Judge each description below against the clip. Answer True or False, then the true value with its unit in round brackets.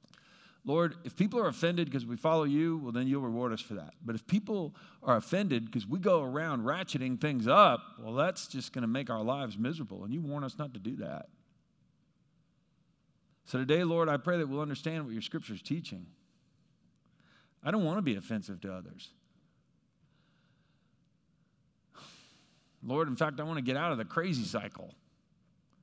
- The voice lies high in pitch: False (150 Hz)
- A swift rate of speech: False (180 wpm)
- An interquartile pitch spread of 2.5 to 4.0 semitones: False (4.6 semitones)